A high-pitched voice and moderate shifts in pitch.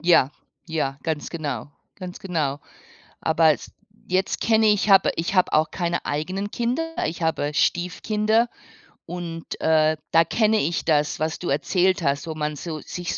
No: medium, 170 Hz; average, 3.7 semitones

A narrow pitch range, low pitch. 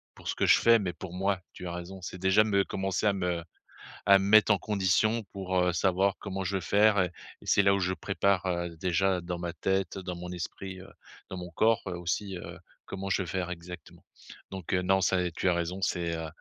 Yes: narrow, 1.7 semitones; very low, 95 Hz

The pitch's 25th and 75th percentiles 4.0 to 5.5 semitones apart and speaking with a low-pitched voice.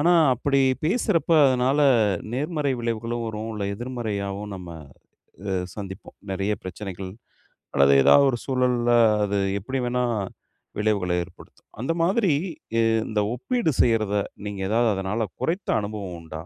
Yes: average, 4.7 semitones; low, 115 Hz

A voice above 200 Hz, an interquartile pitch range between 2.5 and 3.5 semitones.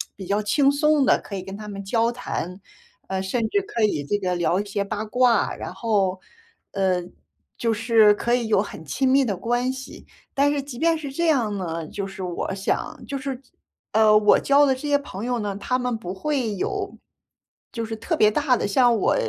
No: high, 220 Hz; average, 4.9 semitones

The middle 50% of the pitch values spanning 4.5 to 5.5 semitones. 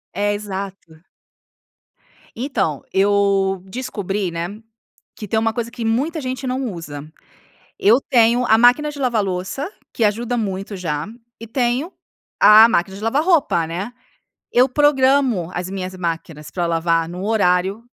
Yes: average, 5.1 semitones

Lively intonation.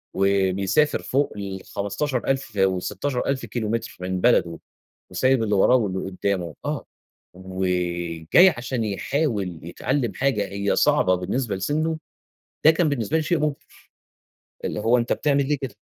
Yes: wide, 6.5 semitones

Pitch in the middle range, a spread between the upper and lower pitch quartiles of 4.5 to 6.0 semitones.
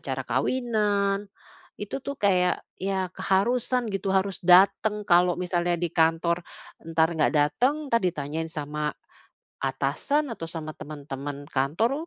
Yes: medium, 180 Hz; average, 5.0 semitones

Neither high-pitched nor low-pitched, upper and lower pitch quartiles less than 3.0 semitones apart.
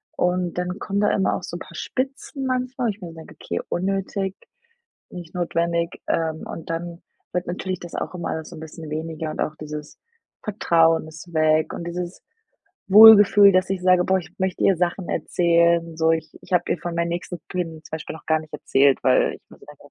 Yes: medium, 175 Hz; narrow, 2.5 semitones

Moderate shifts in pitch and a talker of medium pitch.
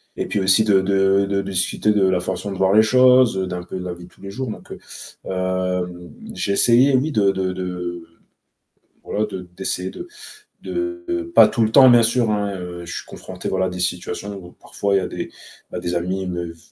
No: average, 3.1 semitones; very low, 95 Hz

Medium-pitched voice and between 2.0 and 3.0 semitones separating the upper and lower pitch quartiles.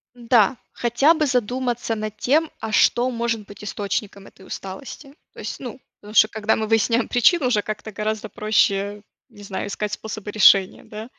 No: high, 220 Hz; average, 2.7 semitones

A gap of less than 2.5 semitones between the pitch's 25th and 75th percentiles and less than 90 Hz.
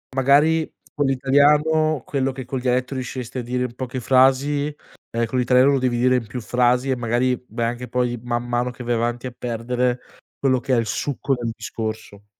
No: narrow, 1.8 semitones; low, 125 Hz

